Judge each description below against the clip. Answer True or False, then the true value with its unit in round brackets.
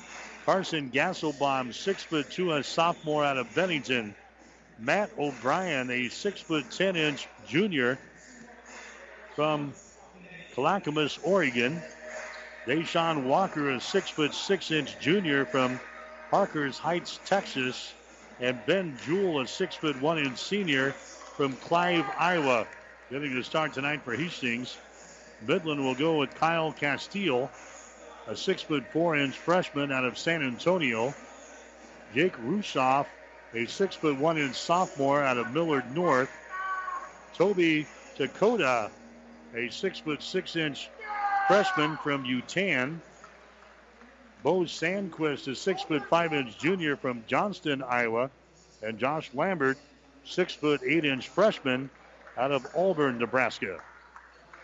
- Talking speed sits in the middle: False (100 wpm)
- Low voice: False (150 Hz)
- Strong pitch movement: False (4.8 semitones)